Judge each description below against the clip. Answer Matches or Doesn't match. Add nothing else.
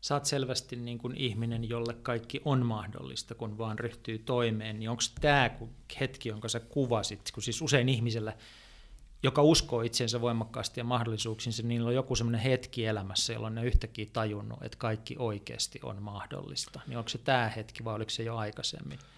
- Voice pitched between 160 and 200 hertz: Doesn't match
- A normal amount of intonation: Doesn't match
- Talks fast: Matches